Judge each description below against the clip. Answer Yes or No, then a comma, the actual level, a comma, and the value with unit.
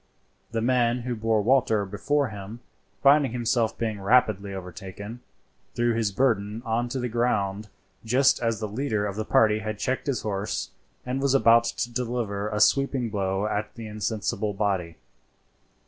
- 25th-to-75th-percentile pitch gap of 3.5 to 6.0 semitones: No, average, 3.0 semitones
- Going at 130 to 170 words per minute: Yes, average, 160 wpm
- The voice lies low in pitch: Yes, low, 110 Hz